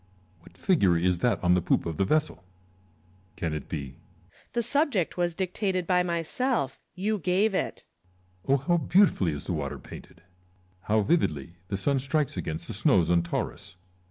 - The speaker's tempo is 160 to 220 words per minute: Yes, average, 175 wpm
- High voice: No, medium, 140 Hz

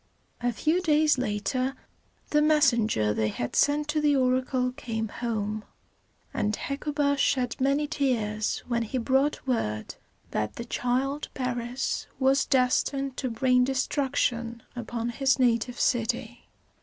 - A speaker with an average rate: No, slow, 130 wpm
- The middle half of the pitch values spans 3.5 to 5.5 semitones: No, average, 3.0 semitones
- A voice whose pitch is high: Yes, very high, 250 Hz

